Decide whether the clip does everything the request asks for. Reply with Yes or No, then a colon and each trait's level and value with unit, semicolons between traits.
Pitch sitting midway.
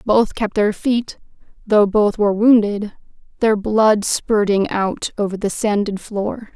No: high, 210 Hz